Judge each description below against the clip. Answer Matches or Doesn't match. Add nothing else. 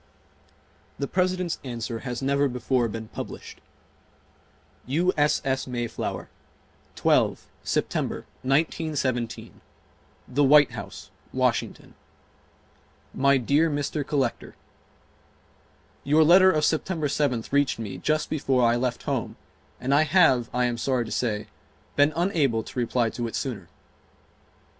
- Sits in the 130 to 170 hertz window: Matches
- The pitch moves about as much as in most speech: Matches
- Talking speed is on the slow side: Matches